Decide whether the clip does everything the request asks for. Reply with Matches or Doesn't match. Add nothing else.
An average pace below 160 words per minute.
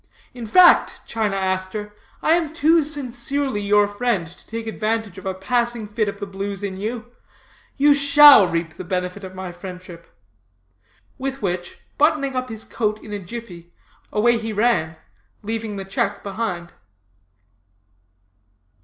Matches